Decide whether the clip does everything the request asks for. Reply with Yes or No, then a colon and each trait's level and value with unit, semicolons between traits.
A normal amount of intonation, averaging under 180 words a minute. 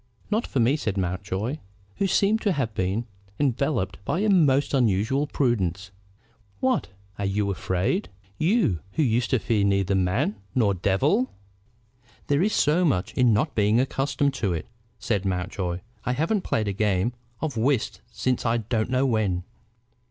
No: wide, 6.4 semitones; average, 160 wpm